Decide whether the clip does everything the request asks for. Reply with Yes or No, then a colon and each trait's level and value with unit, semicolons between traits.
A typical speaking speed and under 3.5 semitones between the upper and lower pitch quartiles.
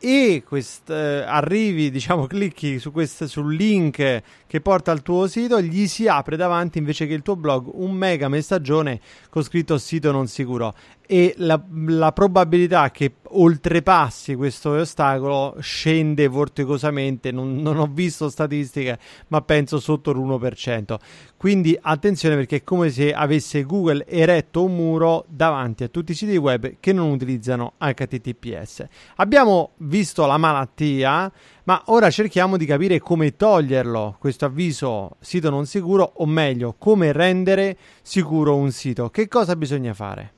No: average, 145 wpm; average, 4.3 semitones